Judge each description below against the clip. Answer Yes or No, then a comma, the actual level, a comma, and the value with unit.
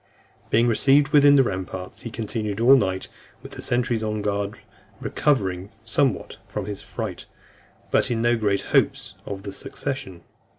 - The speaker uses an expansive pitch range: No, average, 4.3 semitones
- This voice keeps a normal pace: Yes, average, 155 wpm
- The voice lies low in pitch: Yes, low, 110 Hz